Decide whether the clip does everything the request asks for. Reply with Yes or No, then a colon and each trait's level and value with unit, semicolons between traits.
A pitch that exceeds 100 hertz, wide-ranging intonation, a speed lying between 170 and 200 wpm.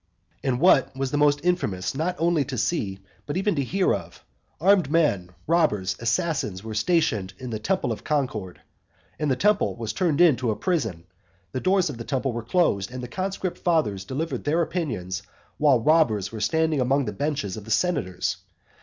Yes: low, 135 Hz; wide, 7.3 semitones; average, 180 wpm